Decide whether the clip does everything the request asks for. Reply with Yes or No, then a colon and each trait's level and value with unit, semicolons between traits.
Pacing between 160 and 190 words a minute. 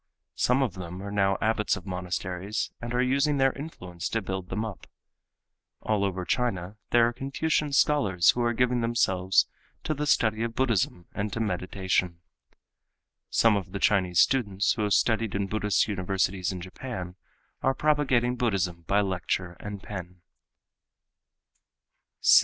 No: average, 150 wpm